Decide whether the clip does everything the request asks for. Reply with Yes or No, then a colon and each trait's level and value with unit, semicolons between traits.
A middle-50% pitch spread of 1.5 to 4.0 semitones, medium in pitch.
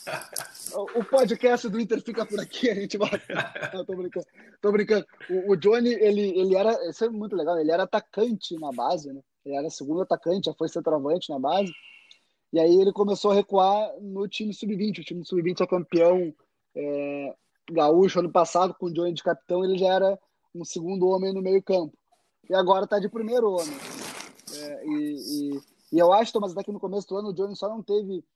No: average, 3.3 semitones; high, 195 Hz